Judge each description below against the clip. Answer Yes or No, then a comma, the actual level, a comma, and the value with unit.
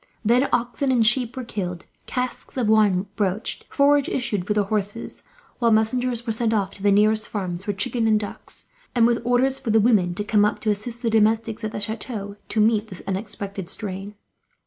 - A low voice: No, high, 215 Hz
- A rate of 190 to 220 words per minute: Yes, average, 200 wpm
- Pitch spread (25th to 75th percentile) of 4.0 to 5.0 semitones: No, narrow, 2.6 semitones